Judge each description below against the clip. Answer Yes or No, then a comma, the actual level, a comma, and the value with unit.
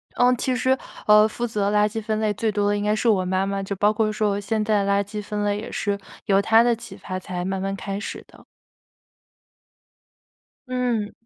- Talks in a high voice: Yes, high, 210 Hz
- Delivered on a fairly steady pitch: Yes, narrow, 1.8 semitones